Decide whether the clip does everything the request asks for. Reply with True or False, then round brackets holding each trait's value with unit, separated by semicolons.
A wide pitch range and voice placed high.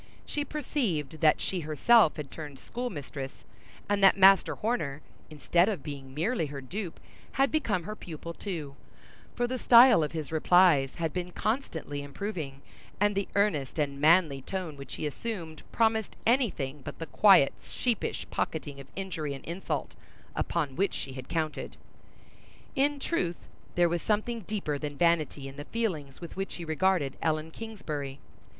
False (6.0 semitones; 170 Hz)